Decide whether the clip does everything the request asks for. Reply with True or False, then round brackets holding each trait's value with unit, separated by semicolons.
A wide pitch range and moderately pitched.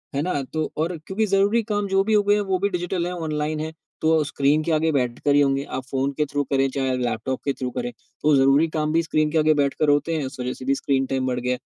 False (3.7 semitones; 150 Hz)